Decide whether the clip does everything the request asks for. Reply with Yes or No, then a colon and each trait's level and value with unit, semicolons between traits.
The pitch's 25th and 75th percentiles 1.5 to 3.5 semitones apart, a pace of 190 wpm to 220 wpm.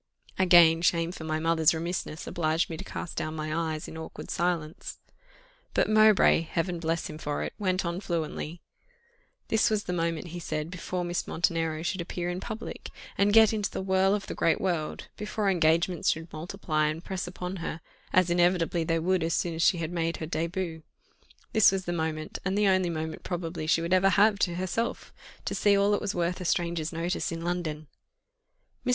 Yes: narrow, 2.4 semitones; average, 195 wpm